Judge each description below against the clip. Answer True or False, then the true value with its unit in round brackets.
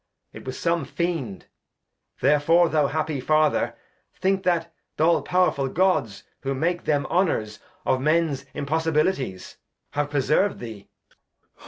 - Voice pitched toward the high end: False (155 Hz)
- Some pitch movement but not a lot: True (3.9 semitones)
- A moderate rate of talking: False (125 wpm)